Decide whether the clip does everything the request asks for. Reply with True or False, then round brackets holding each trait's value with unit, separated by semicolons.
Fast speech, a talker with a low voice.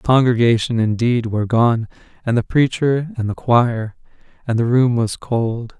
False (165 wpm; 120 Hz)